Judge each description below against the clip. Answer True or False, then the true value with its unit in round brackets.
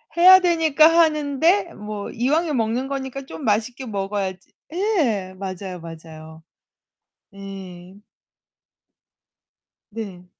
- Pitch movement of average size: False (8.3 semitones)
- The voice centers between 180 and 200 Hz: False (220 Hz)